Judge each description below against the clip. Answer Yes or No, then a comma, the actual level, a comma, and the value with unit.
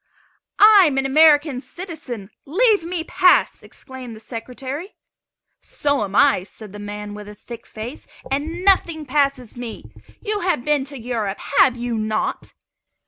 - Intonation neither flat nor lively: No, wide, 5.9 semitones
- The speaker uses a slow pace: No, average, 150 wpm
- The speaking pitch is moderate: No, very high, 265 Hz